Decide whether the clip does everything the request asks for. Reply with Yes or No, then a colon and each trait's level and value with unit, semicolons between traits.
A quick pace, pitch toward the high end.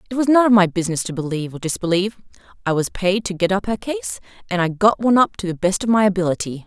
Yes: fast, 260 wpm; high, 195 Hz